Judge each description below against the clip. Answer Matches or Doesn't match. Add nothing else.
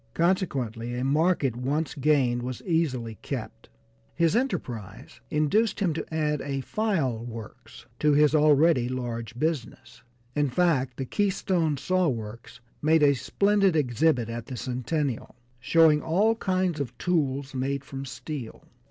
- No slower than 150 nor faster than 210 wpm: Doesn't match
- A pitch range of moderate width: Matches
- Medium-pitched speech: Matches